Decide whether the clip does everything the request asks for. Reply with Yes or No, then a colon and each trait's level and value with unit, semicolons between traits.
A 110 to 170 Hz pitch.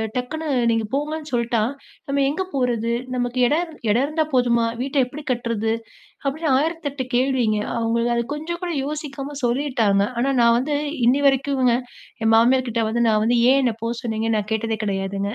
No: high, 245 Hz